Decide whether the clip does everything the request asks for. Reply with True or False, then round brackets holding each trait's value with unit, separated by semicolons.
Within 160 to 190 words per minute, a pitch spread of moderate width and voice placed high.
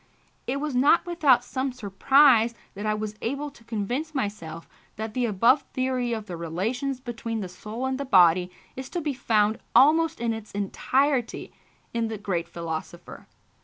True (165 wpm; 4.5 semitones; 235 Hz)